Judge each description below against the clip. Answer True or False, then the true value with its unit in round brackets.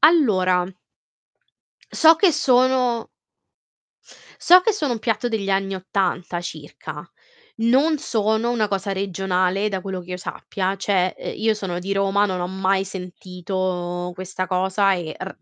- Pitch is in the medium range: False (195 Hz)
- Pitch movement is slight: False (3.3 semitones)